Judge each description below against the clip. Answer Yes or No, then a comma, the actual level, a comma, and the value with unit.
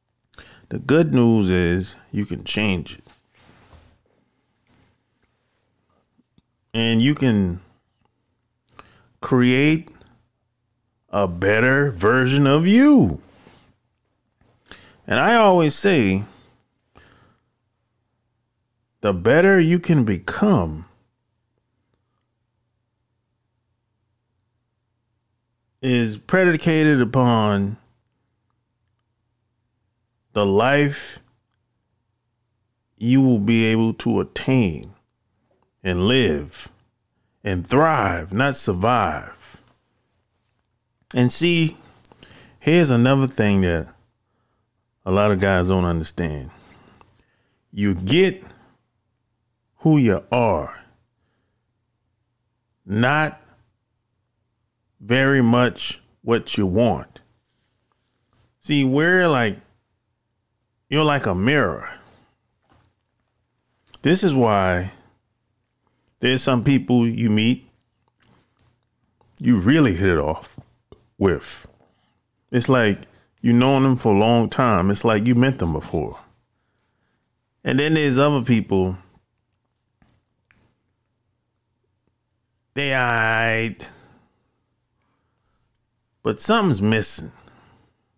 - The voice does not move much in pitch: Yes, narrow, 2.1 semitones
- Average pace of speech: No, slow, 75 wpm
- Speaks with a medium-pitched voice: No, low, 115 Hz